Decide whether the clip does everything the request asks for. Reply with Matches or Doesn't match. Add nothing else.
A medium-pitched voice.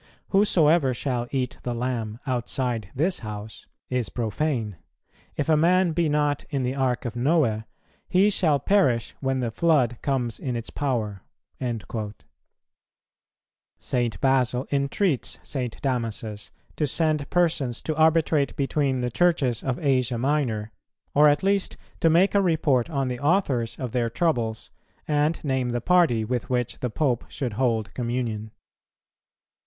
Doesn't match